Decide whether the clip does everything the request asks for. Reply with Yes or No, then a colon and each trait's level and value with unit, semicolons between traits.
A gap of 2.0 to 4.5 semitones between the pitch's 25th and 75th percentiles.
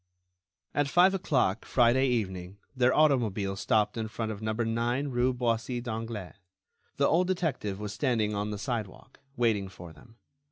Yes: average, 3.7 semitones